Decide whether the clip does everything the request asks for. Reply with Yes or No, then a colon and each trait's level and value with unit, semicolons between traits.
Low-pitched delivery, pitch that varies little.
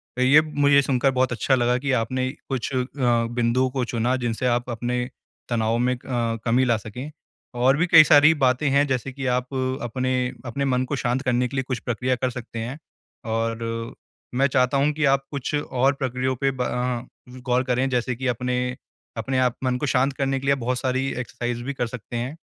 Yes: low, 125 Hz; narrow, 1.9 semitones